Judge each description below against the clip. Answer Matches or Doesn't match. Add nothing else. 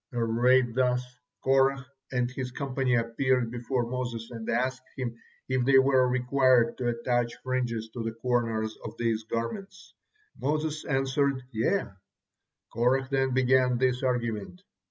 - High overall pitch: Doesn't match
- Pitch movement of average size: Doesn't match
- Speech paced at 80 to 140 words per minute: Matches